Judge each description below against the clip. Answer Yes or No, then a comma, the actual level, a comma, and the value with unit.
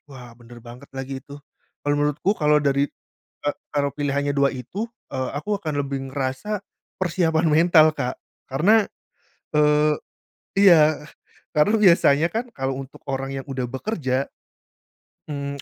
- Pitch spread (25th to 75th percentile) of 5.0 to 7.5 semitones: No, average, 2.8 semitones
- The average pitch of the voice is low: No, medium, 145 Hz